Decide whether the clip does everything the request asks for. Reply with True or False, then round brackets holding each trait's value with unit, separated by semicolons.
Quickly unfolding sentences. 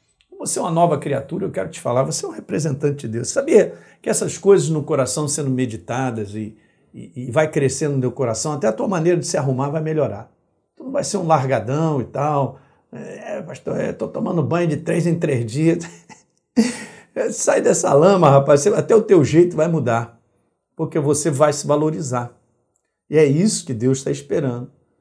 True (195 wpm)